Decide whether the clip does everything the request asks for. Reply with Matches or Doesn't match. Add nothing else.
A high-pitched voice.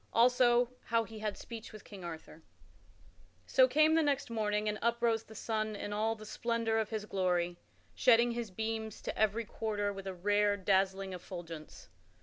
Matches